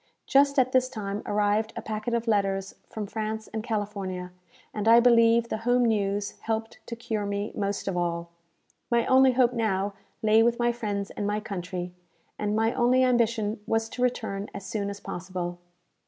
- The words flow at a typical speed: Yes, average, 180 wpm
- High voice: Yes, high, 215 Hz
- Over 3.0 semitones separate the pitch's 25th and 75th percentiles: No, average, 2.7 semitones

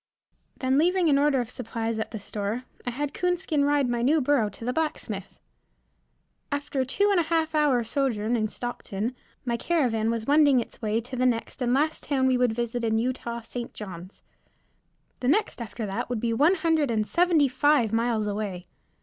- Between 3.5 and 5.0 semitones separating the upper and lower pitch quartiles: Yes, average, 4.4 semitones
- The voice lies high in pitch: Yes, very high, 250 Hz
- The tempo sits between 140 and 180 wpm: No, average, 190 wpm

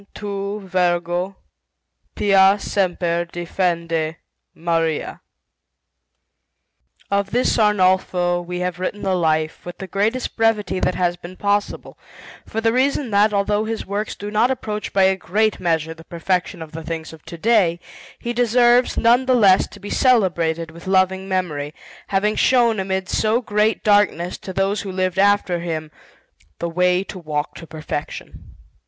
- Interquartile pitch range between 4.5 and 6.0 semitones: No, average, 3.3 semitones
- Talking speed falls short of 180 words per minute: Yes, average, 150 wpm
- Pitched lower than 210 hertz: Yes, high, 190 Hz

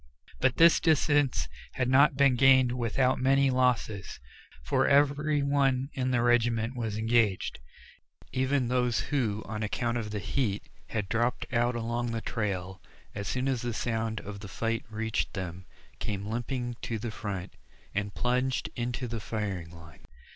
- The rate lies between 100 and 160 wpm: Yes, average, 155 wpm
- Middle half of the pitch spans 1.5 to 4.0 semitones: Yes, average, 3.3 semitones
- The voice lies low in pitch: Yes, low, 120 Hz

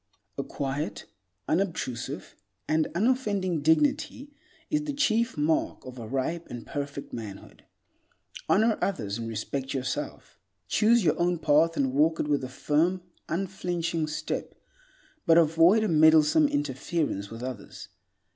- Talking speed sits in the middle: No, slow, 130 wpm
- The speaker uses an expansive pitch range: Yes, wide, 5.8 semitones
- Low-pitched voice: No, medium, 160 Hz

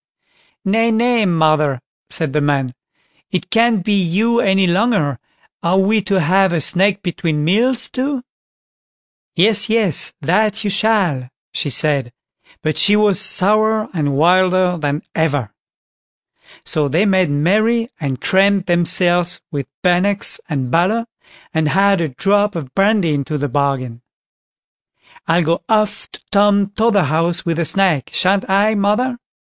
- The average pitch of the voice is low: No, medium, 185 Hz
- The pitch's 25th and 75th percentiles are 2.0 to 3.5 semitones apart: No, average, 5.0 semitones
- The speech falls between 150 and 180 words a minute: No, slow, 135 wpm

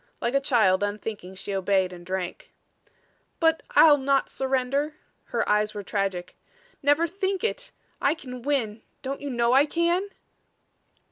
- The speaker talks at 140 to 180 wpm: Yes, average, 145 wpm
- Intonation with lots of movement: Yes, wide, 6.3 semitones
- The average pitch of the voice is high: Yes, very high, 255 Hz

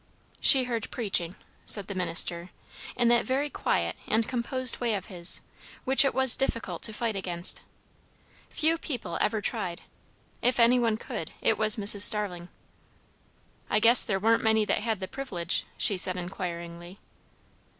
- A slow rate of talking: No, average, 155 wpm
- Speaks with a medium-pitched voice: No, high, 215 Hz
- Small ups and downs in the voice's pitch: No, average, 4.7 semitones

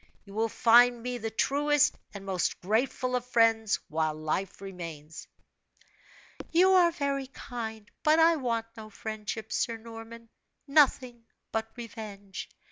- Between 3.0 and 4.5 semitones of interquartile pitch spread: Yes, average, 3.5 semitones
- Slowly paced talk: Yes, slow, 130 wpm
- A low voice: No, high, 225 Hz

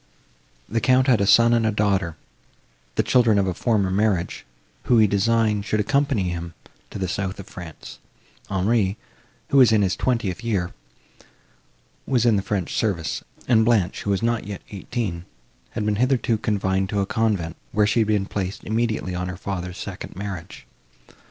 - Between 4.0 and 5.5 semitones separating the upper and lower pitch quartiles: No, average, 3.2 semitones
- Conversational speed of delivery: Yes, average, 175 wpm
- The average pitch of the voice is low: Yes, low, 105 Hz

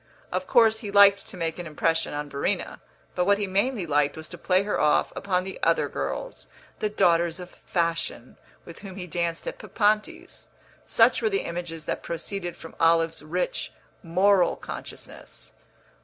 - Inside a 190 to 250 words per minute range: No, average, 170 wpm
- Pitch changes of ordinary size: Yes, average, 3.5 semitones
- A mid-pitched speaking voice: Yes, medium, 180 Hz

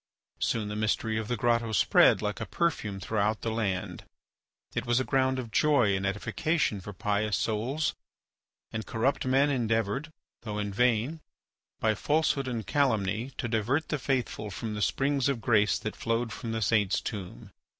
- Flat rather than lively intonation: No, average, 3.8 semitones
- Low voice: Yes, low, 115 Hz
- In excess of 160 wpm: Yes, average, 170 wpm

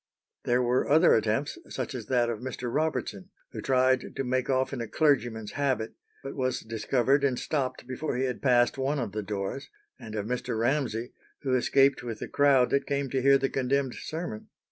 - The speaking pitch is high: No, low, 130 Hz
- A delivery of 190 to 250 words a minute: Yes, average, 195 wpm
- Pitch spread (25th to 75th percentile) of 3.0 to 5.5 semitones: No, narrow, 2.6 semitones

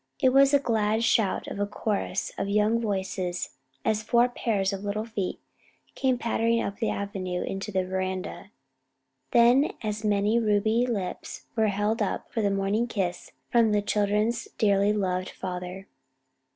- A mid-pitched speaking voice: No, high, 210 Hz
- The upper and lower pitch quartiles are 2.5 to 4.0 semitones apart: Yes, average, 2.8 semitones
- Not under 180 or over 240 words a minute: No, average, 160 wpm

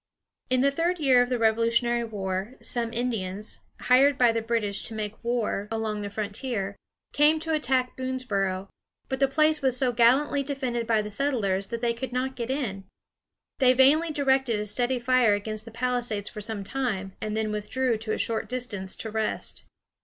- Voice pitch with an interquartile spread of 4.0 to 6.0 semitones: No, average, 3.5 semitones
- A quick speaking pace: No, average, 185 wpm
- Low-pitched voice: No, high, 235 Hz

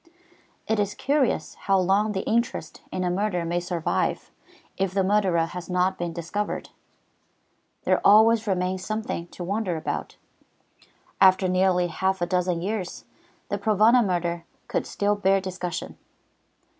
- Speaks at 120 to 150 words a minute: Yes, average, 140 wpm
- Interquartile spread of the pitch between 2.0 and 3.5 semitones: Yes, narrow, 2.6 semitones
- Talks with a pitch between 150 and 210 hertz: Yes, high, 190 Hz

